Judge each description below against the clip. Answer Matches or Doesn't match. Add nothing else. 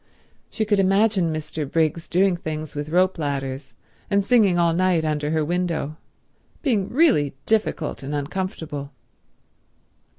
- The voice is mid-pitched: Matches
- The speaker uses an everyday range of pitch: Matches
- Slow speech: Matches